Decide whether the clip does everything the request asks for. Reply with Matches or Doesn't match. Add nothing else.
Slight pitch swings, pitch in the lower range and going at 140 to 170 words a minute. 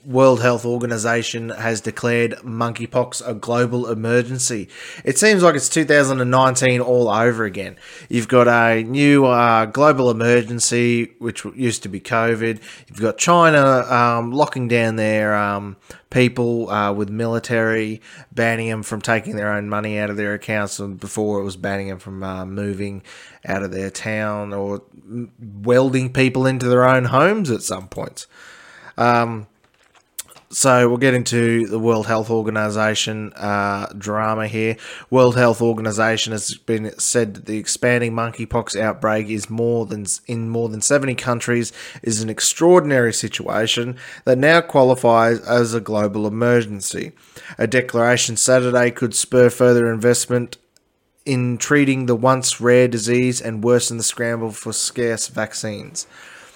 Matches